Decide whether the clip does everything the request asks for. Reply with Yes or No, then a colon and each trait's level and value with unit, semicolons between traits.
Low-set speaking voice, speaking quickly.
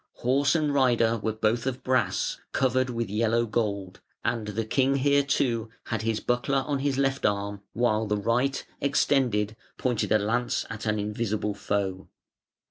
No: low, 115 Hz; average, 160 wpm